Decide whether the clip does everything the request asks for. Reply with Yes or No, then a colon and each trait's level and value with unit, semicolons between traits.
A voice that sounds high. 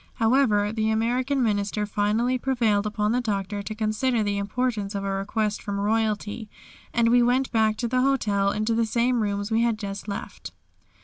Yes: high, 220 Hz